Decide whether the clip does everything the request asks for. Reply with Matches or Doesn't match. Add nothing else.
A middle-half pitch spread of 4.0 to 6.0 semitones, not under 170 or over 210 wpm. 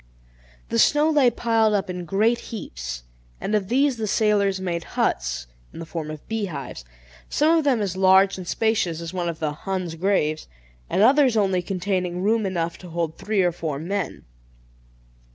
Matches